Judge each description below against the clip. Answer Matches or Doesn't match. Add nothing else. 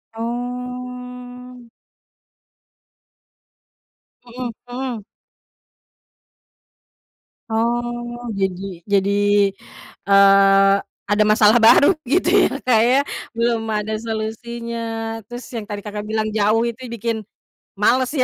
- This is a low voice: Doesn't match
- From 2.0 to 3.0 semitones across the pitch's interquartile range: Matches